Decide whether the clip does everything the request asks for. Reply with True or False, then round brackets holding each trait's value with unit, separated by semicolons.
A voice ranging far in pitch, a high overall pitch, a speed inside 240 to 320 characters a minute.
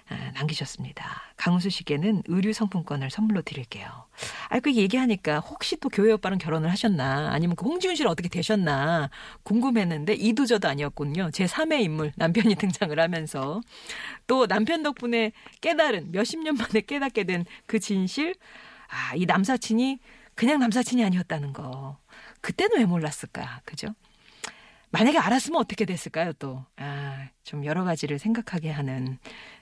False (6.6 semitones; 195 Hz; 335 characters per minute)